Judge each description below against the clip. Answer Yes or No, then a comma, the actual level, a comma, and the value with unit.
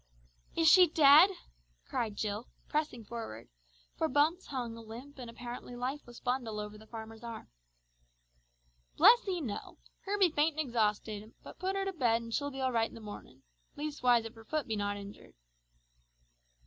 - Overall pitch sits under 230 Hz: No, high, 245 Hz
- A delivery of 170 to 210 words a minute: Yes, average, 175 wpm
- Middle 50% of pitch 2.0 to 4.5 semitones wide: No, average, 5.2 semitones